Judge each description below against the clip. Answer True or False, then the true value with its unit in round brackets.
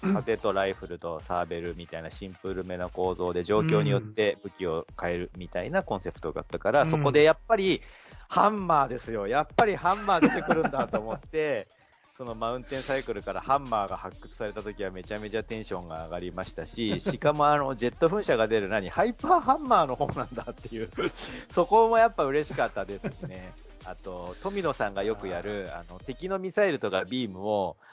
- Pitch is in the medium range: False (110 Hz)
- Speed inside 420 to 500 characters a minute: True (430 characters per minute)